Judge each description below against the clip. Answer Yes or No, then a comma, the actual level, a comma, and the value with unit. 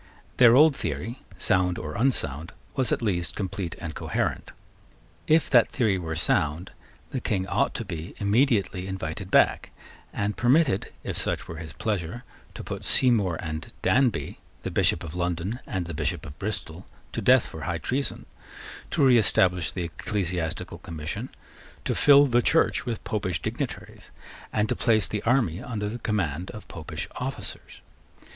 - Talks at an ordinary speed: Yes, average, 155 wpm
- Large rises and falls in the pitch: Yes, wide, 5.9 semitones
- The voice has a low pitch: Yes, very low, 95 Hz